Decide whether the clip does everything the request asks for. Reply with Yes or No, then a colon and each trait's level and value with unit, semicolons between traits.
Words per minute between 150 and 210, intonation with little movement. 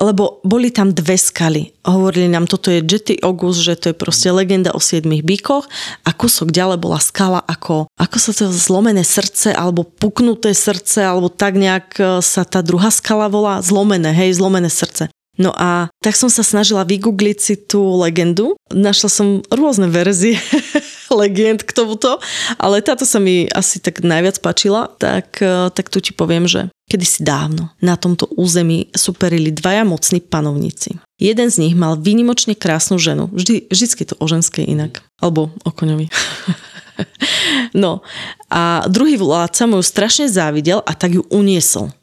No: average, 160 wpm; average, 3.2 semitones